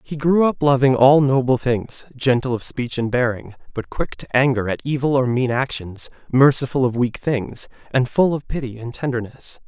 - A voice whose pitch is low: Yes, low, 130 Hz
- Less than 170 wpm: No, average, 190 wpm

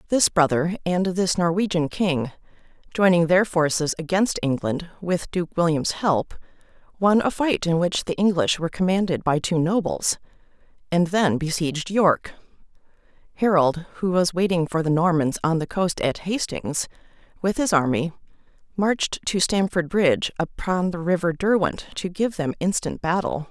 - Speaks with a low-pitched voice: No, medium, 175 Hz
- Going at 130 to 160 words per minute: Yes, average, 150 wpm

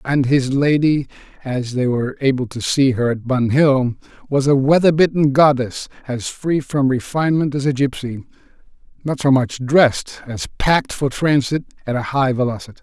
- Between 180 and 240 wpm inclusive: No, average, 170 wpm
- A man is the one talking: Yes, male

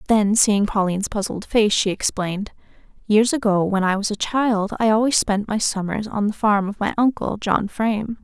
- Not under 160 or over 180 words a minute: No, average, 195 wpm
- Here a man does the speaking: No, female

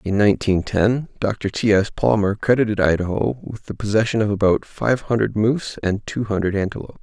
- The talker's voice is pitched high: No, low, 105 Hz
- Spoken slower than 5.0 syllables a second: No, 5.5 syllables/s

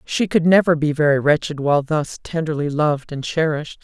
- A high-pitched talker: No, medium, 155 Hz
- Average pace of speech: Yes, average, 190 wpm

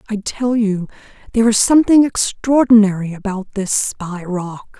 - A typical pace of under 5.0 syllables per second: Yes, 4.6 syllables/s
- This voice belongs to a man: No, female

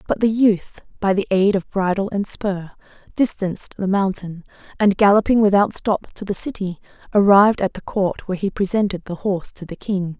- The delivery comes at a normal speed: Yes, average, 190 wpm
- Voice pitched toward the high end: Yes, high, 195 Hz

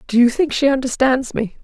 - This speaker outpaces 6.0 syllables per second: No, 5.5 syllables/s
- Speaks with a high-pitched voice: Yes, very high, 255 Hz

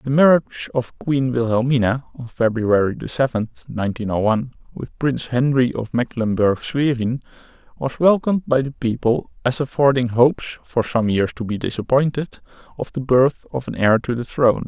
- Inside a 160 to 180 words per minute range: Yes, average, 165 wpm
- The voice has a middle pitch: No, low, 125 Hz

